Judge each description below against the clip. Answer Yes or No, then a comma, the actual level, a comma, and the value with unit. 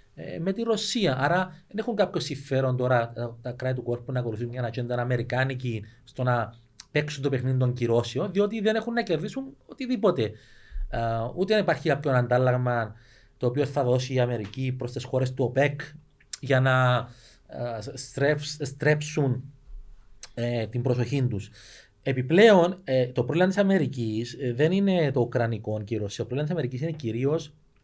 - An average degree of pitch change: Yes, average, 4.0 semitones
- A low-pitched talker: Yes, low, 130 Hz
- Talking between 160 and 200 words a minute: No, average, 150 wpm